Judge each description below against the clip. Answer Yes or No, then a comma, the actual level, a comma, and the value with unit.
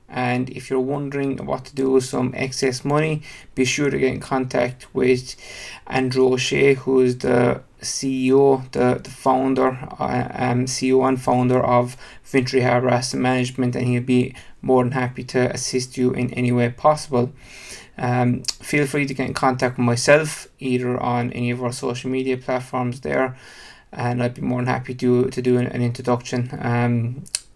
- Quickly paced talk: No, average, 175 wpm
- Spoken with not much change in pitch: Yes, narrow, 1.1 semitones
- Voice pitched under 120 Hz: No, low, 130 Hz